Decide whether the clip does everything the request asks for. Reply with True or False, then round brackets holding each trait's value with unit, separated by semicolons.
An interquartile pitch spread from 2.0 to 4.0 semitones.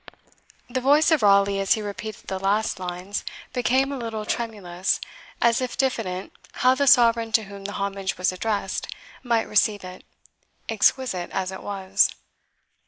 True (3.5 semitones)